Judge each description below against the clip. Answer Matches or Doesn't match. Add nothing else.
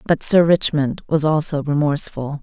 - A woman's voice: Matches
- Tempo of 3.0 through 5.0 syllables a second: Matches